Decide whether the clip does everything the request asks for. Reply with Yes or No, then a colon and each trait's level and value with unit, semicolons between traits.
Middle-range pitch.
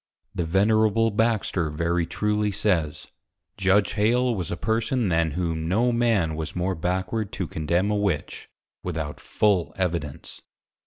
No: very low, 95 Hz